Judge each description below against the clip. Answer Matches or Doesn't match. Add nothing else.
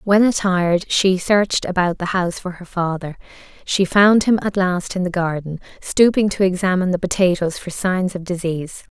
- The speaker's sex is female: Matches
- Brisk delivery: Doesn't match